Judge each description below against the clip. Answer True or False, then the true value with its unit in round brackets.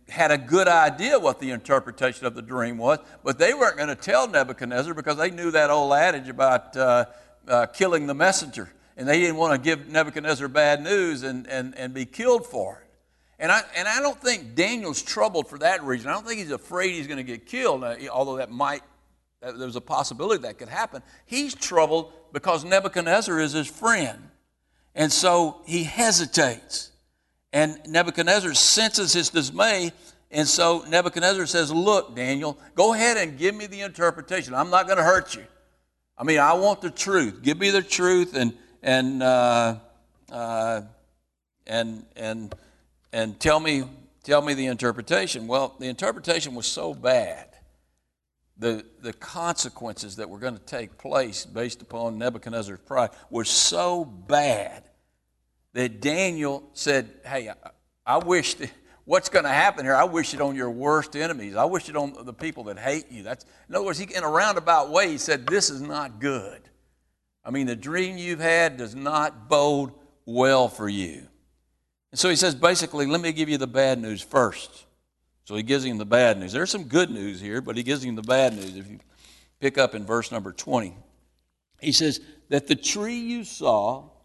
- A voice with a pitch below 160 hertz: True (140 Hz)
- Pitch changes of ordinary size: False (6.3 semitones)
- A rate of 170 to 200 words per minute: True (185 wpm)